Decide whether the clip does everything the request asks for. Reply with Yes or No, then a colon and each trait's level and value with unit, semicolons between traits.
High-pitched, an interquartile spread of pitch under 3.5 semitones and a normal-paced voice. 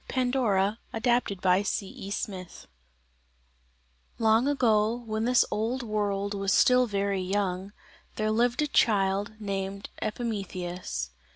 No: high, 210 Hz; average, 3.1 semitones; slow, 115 wpm